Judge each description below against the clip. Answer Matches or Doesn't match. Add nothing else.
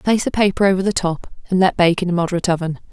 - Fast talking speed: Matches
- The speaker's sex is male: Doesn't match